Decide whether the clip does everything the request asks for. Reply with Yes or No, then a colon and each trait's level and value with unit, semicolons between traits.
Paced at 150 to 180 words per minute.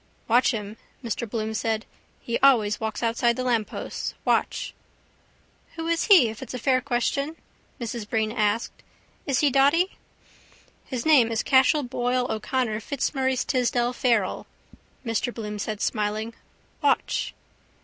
No: slow, 135 wpm